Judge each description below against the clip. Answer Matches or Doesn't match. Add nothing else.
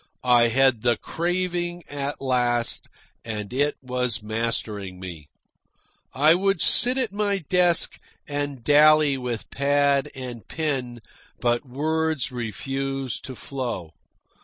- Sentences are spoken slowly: Matches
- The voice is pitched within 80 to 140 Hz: Matches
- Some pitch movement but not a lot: Matches